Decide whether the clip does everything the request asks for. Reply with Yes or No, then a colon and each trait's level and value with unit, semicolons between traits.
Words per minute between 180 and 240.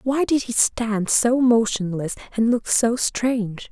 No: average, 160 wpm